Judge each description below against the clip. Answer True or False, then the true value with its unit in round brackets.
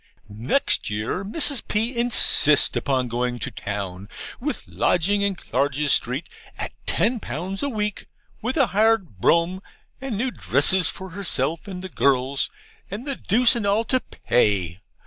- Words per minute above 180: False (150 wpm)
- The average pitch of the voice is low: False (185 Hz)